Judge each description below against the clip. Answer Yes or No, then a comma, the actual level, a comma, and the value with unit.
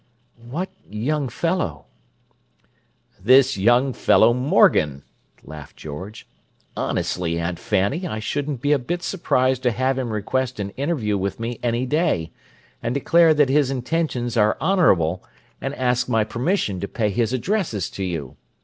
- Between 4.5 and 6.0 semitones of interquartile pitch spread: Yes, wide, 5.6 semitones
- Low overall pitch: Yes, low, 120 Hz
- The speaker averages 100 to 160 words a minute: Yes, average, 145 wpm